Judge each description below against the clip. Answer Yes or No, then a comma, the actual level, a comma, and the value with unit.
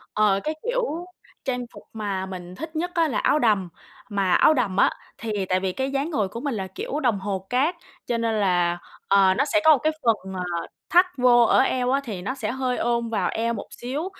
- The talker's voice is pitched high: Yes, high, 235 Hz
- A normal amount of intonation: No, wide, 5.9 semitones